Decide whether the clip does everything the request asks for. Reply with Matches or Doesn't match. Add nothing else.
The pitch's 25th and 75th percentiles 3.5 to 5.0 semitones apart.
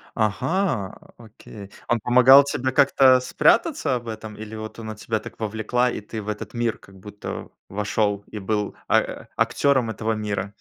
Doesn't match